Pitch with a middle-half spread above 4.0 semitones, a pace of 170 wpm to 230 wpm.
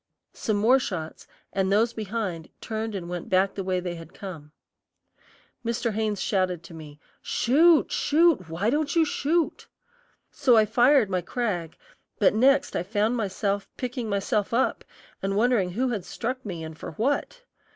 No: average, 5.0 semitones; average, 160 wpm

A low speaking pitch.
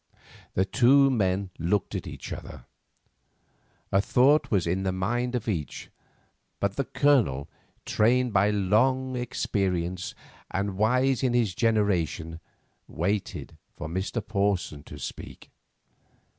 Yes: low, 100 Hz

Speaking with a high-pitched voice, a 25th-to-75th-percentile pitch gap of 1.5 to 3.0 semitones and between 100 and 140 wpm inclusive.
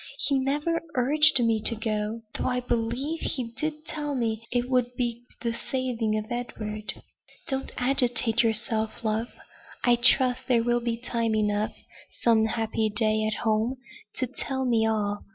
No: high, 235 Hz; narrow, 2.5 semitones; average, 155 wpm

